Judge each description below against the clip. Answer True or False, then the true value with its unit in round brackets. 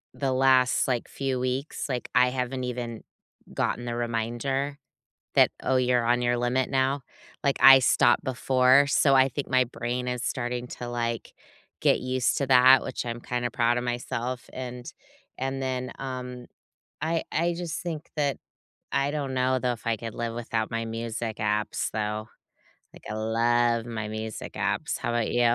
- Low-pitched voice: True (125 Hz)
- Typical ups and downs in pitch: False (1.9 semitones)